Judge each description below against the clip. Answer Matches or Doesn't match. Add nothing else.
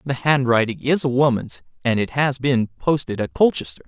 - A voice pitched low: Matches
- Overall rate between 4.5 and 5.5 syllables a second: Matches